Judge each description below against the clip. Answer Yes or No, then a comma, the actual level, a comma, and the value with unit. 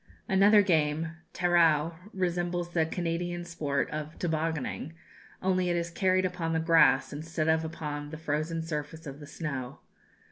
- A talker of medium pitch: Yes, medium, 165 Hz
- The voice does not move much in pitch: Yes, narrow, 2.3 semitones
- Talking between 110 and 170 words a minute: Yes, average, 150 wpm